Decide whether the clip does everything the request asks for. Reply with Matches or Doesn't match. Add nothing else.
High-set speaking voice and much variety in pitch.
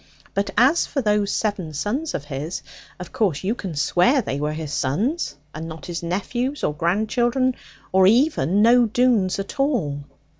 Matches